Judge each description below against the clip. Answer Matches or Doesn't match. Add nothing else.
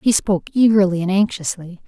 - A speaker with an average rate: Matches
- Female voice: Matches